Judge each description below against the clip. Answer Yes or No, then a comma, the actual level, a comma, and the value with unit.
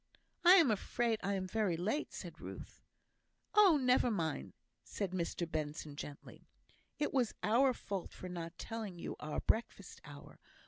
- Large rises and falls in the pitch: Yes, wide, 6.3 semitones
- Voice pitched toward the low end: No, high, 200 Hz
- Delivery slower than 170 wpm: Yes, average, 150 wpm